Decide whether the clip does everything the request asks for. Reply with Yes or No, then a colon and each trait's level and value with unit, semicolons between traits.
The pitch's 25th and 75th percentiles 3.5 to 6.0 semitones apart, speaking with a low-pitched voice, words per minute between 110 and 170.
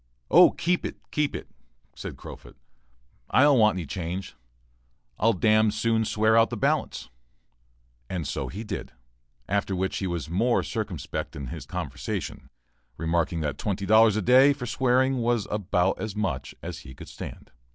Yes: average, 4.4 semitones; low, 105 Hz; average, 160 wpm